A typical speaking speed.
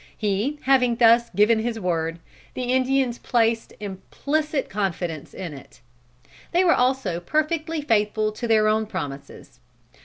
No: slow, 130 wpm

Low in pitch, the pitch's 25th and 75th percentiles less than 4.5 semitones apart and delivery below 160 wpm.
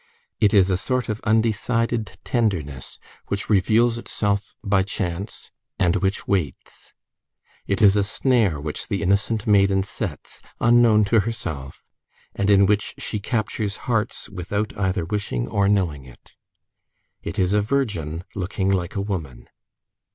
Yes: low, 100 Hz; average, 2.8 semitones; average, 140 wpm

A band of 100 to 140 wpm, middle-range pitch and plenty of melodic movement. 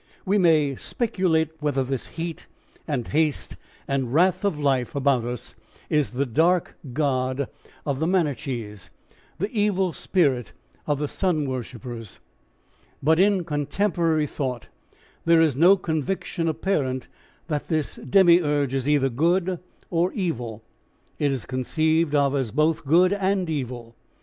No: slow, 135 wpm; medium, 150 Hz; average, 4.6 semitones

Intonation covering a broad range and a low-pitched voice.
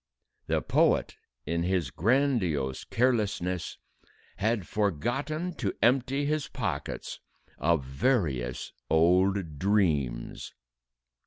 Yes: wide, 7.1 semitones; very low, 95 Hz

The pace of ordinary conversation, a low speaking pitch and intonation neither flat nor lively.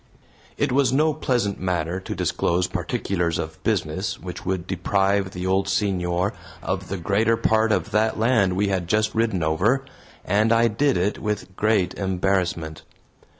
Yes: average, 155 wpm; low, 100 Hz; average, 3.4 semitones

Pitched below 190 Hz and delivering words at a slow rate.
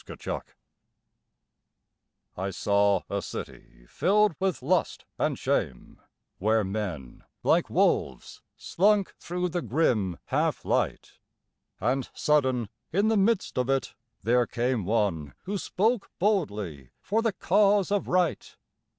Yes: low, 135 Hz; slow, 120 wpm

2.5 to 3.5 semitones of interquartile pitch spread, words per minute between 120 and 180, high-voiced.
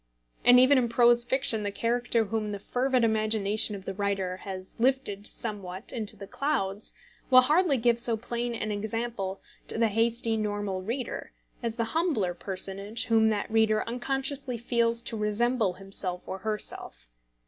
Yes: average, 2.9 semitones; average, 160 wpm; high, 225 Hz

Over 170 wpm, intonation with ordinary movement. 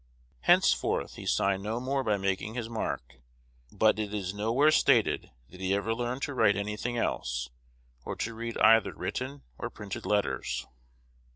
No: average, 165 wpm; average, 3.4 semitones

